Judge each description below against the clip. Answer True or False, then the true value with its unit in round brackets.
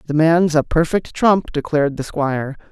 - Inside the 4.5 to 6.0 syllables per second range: True (5.0 syllables/s)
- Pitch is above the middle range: False (155 Hz)